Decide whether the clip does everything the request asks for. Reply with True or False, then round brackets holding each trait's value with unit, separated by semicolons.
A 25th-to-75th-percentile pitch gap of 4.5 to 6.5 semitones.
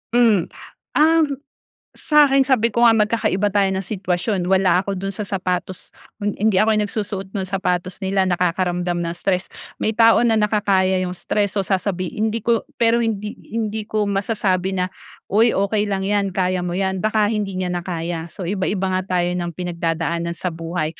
False (2.8 semitones)